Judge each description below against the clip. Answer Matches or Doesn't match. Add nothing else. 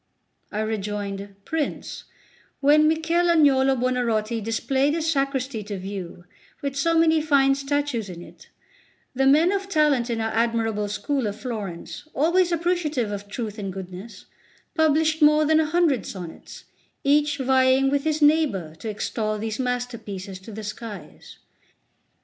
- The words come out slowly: Doesn't match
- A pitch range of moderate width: Doesn't match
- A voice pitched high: Matches